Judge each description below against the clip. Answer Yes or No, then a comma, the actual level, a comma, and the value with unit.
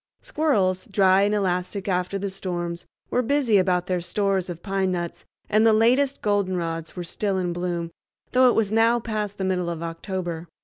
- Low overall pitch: No, high, 190 Hz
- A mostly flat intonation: No, average, 3.1 semitones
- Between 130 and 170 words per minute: No, average, 180 wpm